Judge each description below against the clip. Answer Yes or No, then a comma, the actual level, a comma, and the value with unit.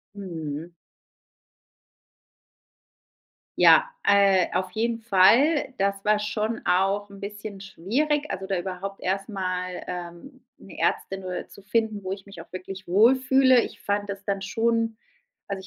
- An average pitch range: Yes, average, 3.2 semitones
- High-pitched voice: Yes, high, 200 Hz